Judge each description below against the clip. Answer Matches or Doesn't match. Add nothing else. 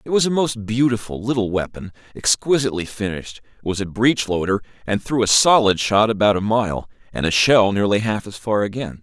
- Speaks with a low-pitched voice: Matches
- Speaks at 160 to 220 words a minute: Matches